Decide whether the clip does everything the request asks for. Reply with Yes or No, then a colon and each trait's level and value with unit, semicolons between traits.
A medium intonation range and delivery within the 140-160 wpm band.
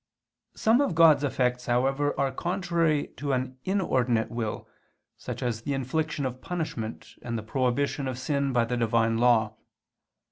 Yes: average, 3.6 semitones; average, 150 wpm